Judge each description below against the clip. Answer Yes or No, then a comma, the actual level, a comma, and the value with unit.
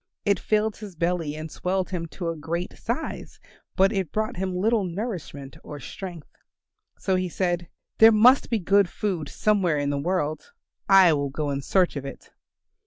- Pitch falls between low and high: Yes, medium, 180 Hz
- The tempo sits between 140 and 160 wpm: No, average, 175 wpm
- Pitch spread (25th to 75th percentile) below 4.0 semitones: No, average, 4.3 semitones